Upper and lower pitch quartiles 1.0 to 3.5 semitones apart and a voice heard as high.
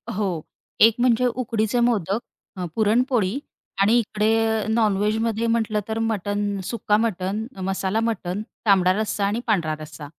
Yes: narrow, 2.5 semitones; high, 215 Hz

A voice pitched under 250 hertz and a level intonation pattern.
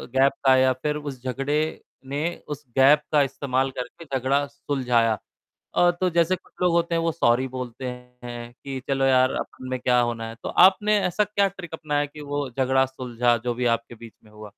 No: low, 135 Hz; average, 3.2 semitones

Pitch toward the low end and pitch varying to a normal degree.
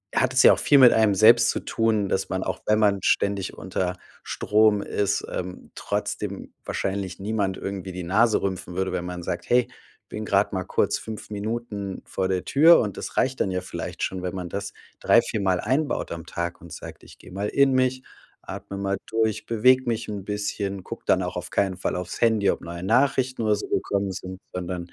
Yes: low, 100 Hz; average, 3.1 semitones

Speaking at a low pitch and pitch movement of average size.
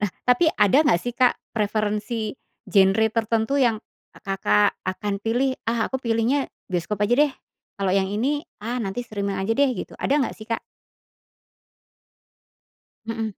No: high, 225 Hz; average, 3.3 semitones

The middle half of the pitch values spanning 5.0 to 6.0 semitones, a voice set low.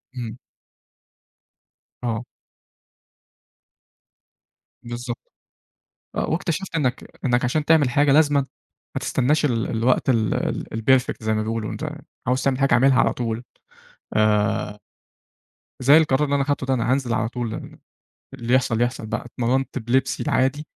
No: average, 2.9 semitones; low, 125 Hz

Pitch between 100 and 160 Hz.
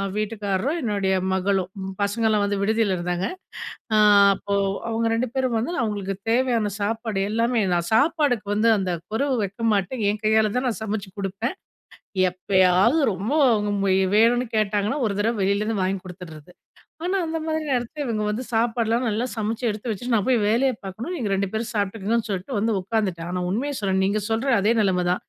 No: high, 215 Hz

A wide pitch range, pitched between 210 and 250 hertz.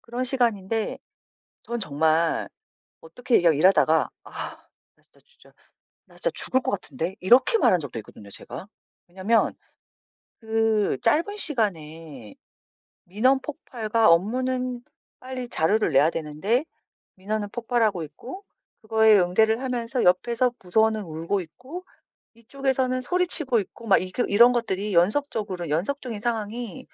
Yes: wide, 5.7 semitones; high, 220 Hz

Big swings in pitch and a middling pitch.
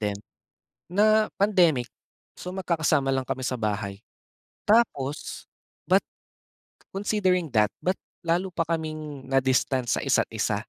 Yes: wide, 5.9 semitones; medium, 155 Hz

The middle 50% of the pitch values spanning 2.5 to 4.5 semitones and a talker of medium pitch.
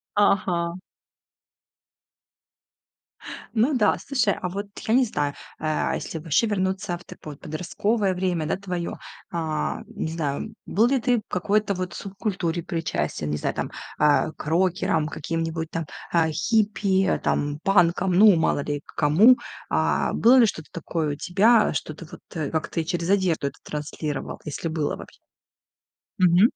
Yes: average, 4.2 semitones; medium, 175 Hz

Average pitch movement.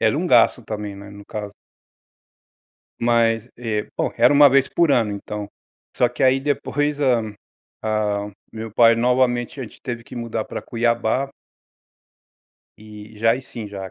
Yes: average, 3.0 semitones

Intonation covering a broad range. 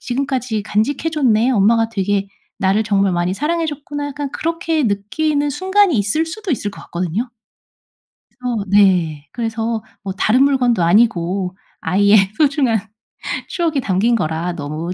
Yes: wide, 6.6 semitones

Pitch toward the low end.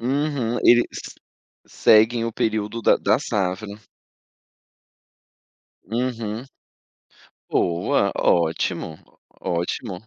Yes: low, 110 Hz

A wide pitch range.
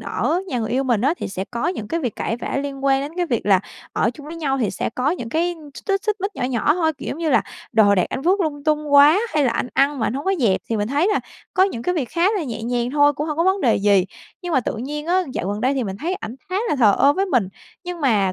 Yes: wide, 5.8 semitones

